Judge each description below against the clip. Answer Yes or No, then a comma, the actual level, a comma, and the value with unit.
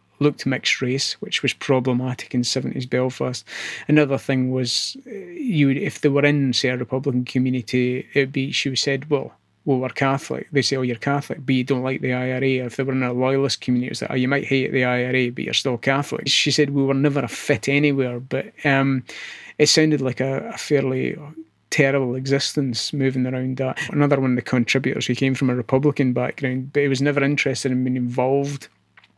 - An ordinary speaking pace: No, fast, 215 wpm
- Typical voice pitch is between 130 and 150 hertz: Yes, low, 135 Hz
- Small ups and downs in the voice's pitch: Yes, narrow, 1.8 semitones